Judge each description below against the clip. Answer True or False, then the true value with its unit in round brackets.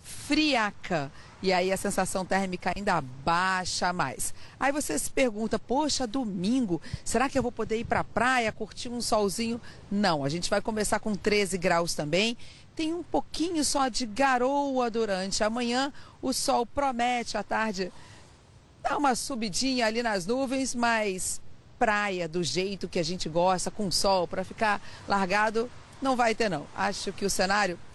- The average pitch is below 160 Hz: False (215 Hz)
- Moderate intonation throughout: True (4.6 semitones)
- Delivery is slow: False (165 wpm)